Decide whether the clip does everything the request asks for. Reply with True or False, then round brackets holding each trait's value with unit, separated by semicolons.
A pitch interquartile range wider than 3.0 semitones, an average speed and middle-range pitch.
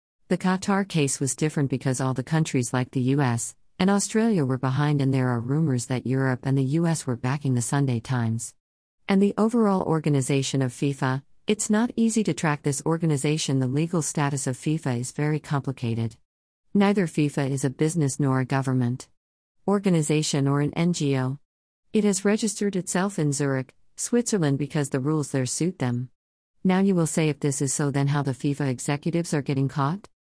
True (4.0 semitones; 180 wpm; 145 Hz)